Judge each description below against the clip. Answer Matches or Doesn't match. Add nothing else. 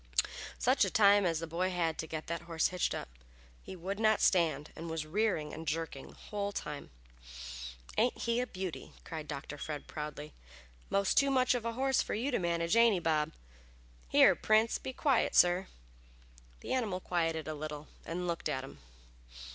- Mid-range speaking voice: Matches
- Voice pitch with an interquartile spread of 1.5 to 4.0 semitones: Doesn't match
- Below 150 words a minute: Doesn't match